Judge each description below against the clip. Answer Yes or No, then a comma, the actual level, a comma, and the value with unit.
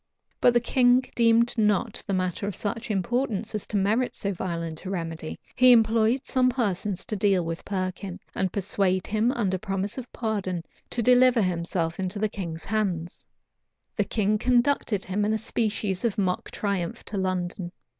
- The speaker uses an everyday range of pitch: Yes, average, 3.6 semitones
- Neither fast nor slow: Yes, average, 170 wpm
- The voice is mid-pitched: No, high, 205 Hz